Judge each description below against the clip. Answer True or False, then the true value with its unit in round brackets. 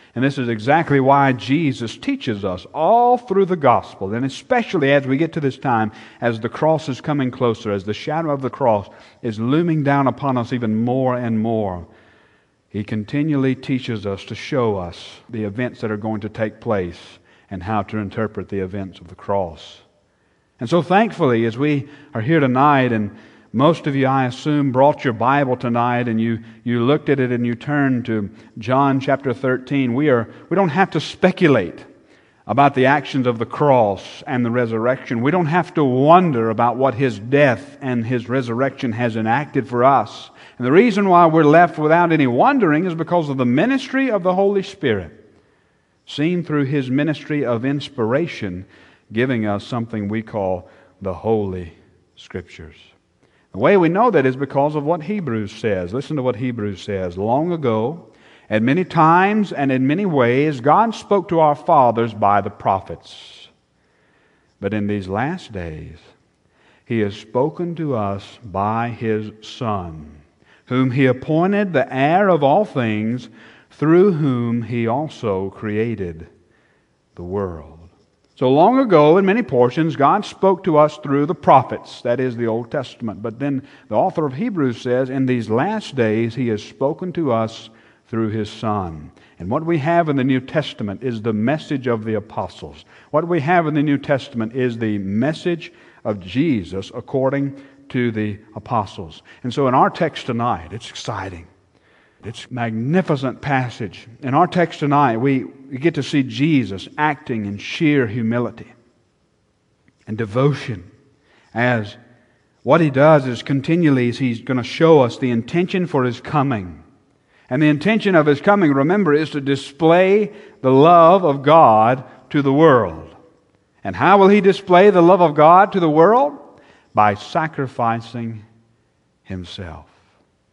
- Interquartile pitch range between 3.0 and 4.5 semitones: False (5.2 semitones)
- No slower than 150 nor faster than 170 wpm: True (165 wpm)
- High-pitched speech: False (125 Hz)